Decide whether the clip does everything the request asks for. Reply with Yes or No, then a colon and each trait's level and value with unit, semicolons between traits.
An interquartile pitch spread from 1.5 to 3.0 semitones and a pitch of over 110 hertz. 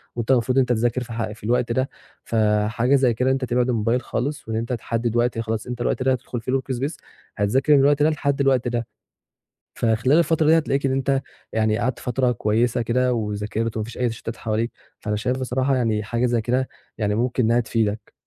Yes: narrow, 2.6 semitones; low, 120 Hz